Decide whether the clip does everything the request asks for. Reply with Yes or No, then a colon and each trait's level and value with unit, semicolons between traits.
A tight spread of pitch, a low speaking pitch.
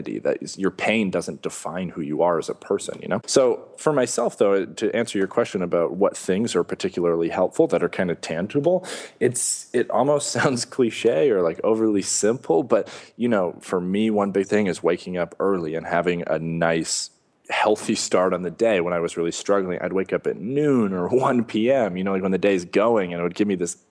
No: average, 4.7 semitones; very low, 95 Hz